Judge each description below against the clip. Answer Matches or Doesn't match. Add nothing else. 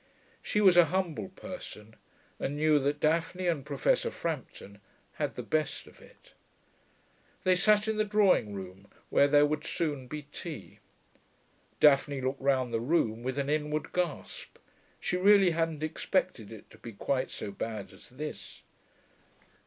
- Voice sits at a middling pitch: Matches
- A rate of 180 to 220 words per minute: Doesn't match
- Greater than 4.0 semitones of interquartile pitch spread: Matches